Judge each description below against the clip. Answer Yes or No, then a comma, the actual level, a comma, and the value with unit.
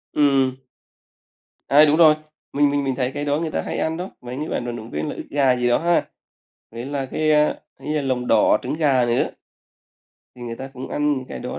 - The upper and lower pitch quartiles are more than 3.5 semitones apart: No, average, 3.2 semitones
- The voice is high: No, low, 135 Hz